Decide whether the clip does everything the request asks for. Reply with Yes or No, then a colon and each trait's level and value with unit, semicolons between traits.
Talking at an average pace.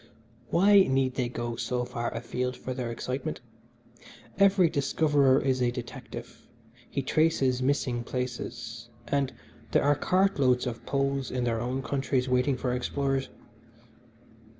No: slow, 130 wpm